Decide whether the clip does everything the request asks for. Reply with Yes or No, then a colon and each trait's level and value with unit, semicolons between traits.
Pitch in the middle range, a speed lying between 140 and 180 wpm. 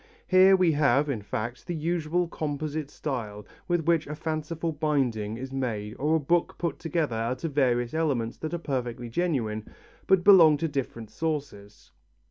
Yes: medium, 150 Hz; average, 165 wpm